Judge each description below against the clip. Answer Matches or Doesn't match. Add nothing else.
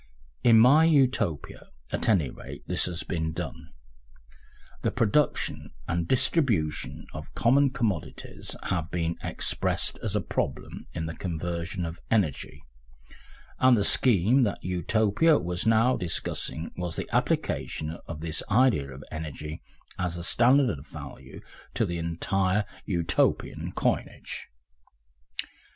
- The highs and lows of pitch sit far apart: Matches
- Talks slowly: Matches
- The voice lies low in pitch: Matches